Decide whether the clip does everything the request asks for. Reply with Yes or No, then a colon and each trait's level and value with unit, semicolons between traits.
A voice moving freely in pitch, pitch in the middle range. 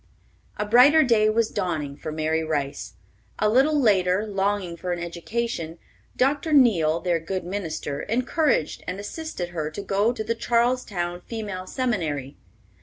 No: wide, 5.8 semitones; high, 195 Hz